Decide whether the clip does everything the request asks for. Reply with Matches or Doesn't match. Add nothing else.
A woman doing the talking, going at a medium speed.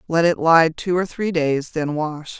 Doesn't match